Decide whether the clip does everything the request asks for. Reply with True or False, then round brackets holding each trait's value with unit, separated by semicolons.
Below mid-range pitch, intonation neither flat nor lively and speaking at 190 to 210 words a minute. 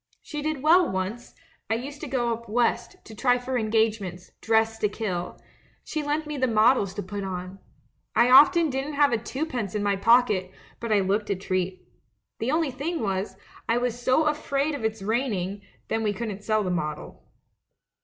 False (225 Hz; 5.0 semitones; 195 wpm)